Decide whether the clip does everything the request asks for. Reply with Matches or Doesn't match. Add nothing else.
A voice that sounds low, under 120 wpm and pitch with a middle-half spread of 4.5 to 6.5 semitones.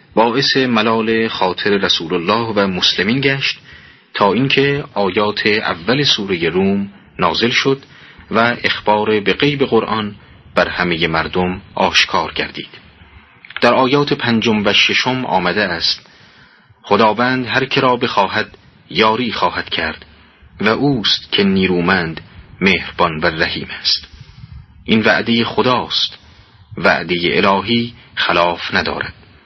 Matches